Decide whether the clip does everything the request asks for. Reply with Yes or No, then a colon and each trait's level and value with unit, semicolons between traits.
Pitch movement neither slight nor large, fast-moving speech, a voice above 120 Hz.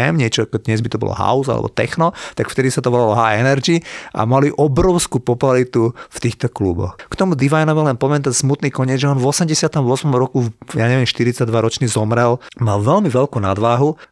Yes: average, 3.7 semitones; fast, 185 wpm; low, 130 Hz